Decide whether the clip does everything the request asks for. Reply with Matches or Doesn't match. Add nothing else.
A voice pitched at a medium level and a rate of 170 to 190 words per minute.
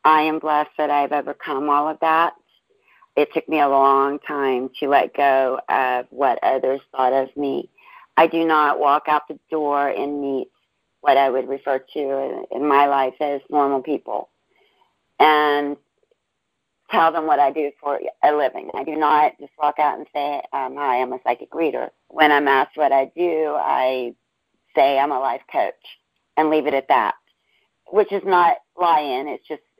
Matches